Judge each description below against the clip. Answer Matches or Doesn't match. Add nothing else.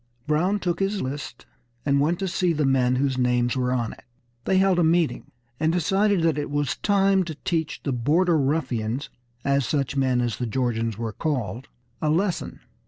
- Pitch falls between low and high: Matches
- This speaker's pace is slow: Doesn't match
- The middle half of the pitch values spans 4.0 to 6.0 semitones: Matches